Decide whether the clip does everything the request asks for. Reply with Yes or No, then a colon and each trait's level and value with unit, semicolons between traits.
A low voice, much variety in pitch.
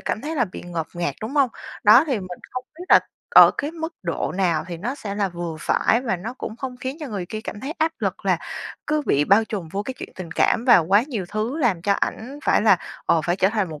No: high, 215 Hz; wide, 6.2 semitones